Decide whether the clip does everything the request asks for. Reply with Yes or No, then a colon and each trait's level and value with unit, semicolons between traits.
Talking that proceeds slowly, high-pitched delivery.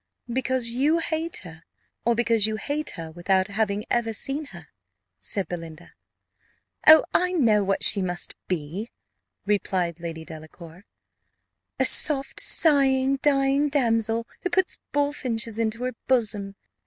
Yes: slow, 130 wpm; high, 225 Hz